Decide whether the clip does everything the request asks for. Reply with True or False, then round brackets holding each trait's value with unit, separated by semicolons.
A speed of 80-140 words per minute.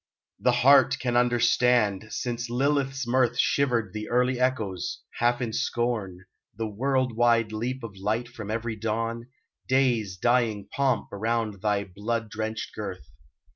True (135 wpm)